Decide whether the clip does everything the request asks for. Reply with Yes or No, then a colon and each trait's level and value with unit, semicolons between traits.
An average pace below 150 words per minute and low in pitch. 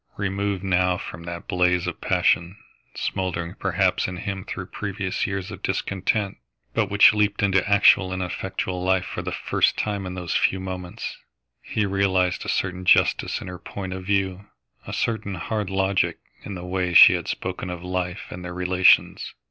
No: average, 175 wpm; very low, 95 Hz